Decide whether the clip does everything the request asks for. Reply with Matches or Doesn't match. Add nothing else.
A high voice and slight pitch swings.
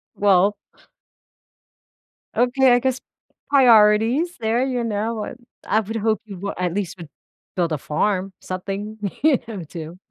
Doesn't match